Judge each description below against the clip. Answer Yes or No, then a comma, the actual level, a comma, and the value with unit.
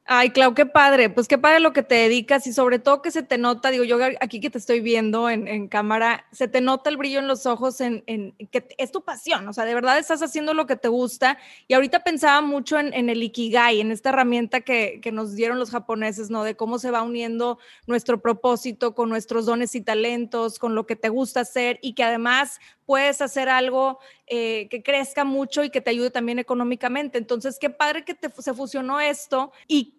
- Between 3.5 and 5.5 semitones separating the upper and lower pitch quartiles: No, average, 2.7 semitones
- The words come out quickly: Yes, fast, 225 wpm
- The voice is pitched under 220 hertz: No, very high, 250 Hz